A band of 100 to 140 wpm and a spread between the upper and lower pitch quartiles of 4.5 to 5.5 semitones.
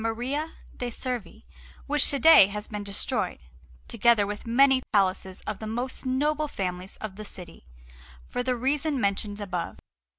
No: average, 155 wpm; average, 4.8 semitones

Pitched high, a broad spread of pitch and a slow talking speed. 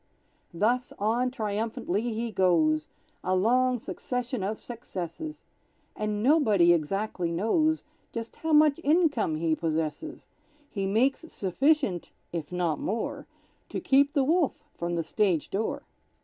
Yes: high, 215 Hz; wide, 6.7 semitones; slow, 125 wpm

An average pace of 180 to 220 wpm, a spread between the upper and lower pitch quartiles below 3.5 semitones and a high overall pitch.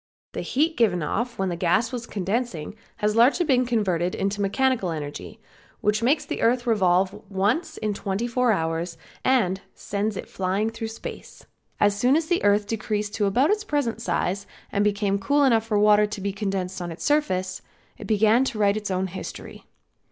No: average, 185 wpm; average, 3.8 semitones; high, 210 Hz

